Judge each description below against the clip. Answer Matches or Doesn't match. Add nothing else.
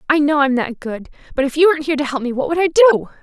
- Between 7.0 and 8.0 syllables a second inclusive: Matches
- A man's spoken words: Doesn't match